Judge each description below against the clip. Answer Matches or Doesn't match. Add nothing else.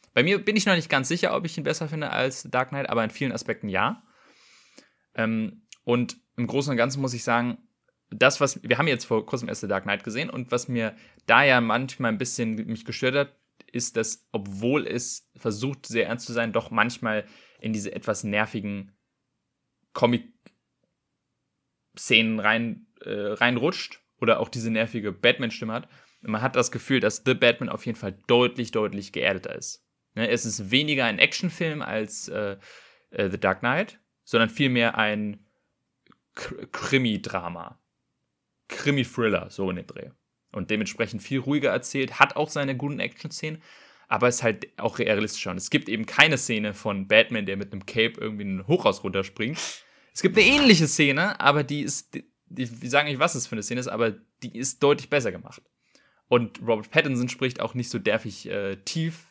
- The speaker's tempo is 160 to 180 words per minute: Matches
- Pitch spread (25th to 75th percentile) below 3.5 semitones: Doesn't match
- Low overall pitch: Matches